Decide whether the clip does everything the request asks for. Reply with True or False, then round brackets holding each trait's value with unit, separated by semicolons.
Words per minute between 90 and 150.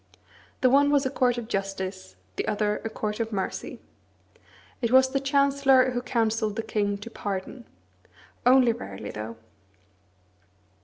True (145 wpm)